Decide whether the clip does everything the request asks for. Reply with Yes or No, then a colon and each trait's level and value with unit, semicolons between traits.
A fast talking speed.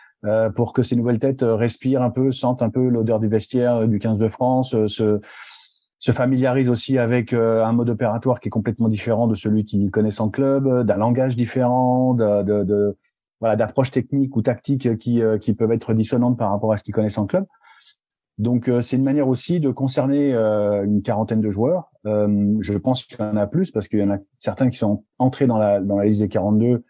Yes: fast, 230 wpm